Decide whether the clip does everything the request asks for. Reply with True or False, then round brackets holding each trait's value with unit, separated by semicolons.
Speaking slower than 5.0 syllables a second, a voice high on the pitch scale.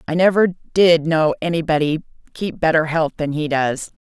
False (4.8 syllables/s; 160 Hz)